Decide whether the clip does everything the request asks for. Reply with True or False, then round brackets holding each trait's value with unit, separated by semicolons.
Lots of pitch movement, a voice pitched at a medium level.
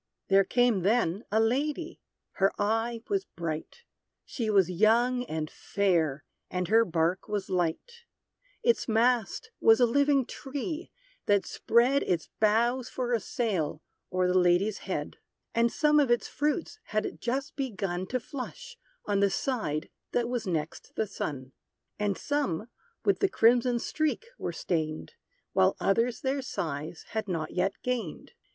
False (5.7 semitones; 225 Hz)